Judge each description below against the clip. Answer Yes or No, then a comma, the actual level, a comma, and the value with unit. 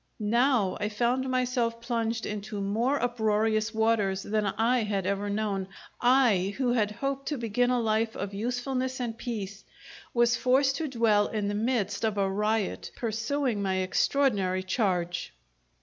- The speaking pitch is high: Yes, high, 220 Hz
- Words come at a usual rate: Yes, average, 150 wpm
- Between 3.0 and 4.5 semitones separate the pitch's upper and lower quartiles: Yes, average, 3.4 semitones